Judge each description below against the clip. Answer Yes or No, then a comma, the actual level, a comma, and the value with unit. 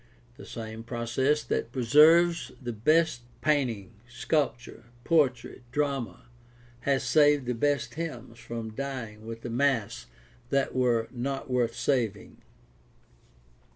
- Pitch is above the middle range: No, low, 125 Hz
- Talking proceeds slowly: Yes, slow, 115 wpm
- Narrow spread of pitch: No, average, 3.6 semitones